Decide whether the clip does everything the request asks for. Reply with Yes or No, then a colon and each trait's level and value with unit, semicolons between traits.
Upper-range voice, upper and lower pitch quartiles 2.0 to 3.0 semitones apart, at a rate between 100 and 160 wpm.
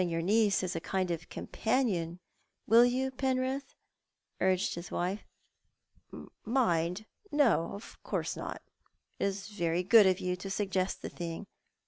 No: high, 195 Hz; average, 4.5 semitones; average, 150 wpm